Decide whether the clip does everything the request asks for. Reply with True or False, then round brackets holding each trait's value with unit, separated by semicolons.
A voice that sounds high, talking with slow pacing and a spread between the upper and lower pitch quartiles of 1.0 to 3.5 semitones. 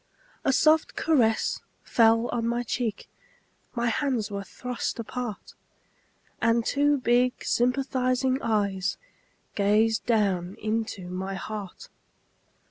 True (230 Hz; 105 wpm; 3.2 semitones)